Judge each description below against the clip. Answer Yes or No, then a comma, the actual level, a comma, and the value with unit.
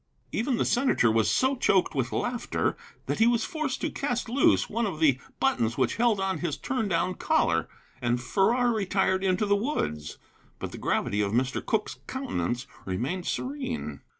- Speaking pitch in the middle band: No, high, 195 Hz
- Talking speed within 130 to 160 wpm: No, average, 175 wpm